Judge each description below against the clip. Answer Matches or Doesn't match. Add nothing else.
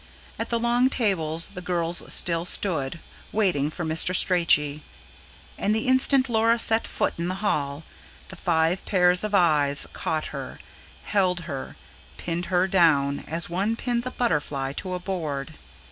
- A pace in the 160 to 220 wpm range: Doesn't match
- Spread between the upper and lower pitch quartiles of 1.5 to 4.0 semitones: Doesn't match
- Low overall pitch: Doesn't match